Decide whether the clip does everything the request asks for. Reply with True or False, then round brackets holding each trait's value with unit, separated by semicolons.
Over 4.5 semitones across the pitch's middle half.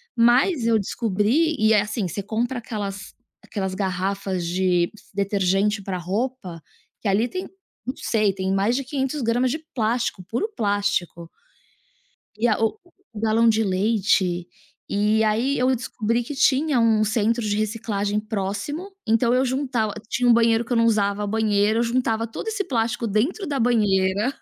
False (3.2 semitones)